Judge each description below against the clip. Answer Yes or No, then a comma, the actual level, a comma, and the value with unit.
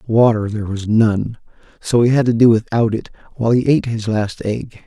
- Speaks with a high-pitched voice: No, low, 115 Hz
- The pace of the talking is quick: Yes, fast, 210 wpm